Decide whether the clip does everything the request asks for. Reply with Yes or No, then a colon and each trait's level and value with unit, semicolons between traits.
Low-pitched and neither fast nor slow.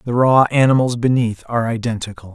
Yes: low, 120 Hz; average, 155 wpm